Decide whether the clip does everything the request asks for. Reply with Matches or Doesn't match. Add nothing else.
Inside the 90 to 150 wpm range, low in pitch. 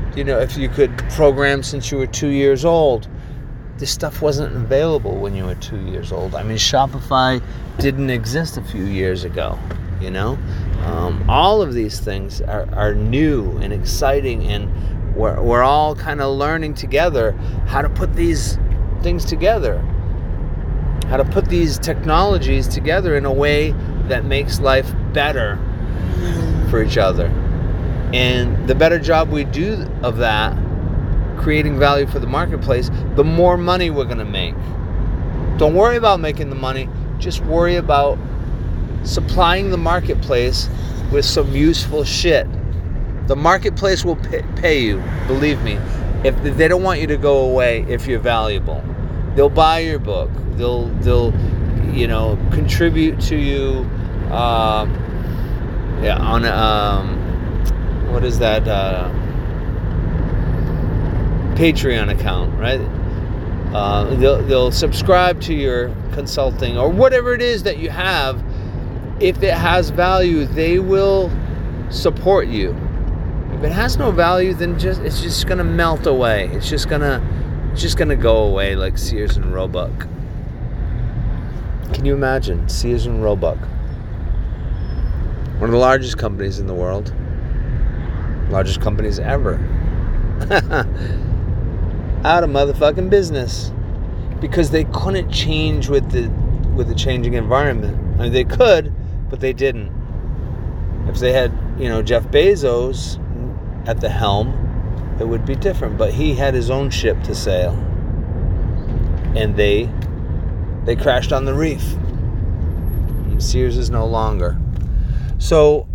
Matches